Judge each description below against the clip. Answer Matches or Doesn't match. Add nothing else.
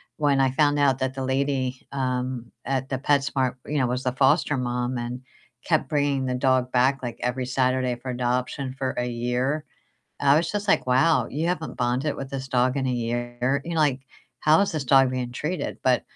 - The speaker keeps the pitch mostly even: Matches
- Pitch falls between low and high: Doesn't match